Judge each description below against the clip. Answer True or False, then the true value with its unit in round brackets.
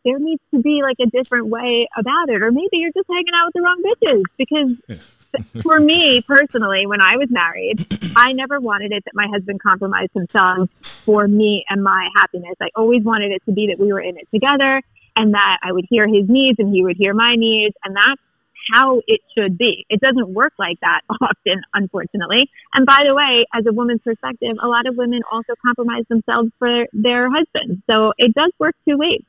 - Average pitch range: True (4.9 semitones)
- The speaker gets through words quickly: True (215 wpm)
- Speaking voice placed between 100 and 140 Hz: False (235 Hz)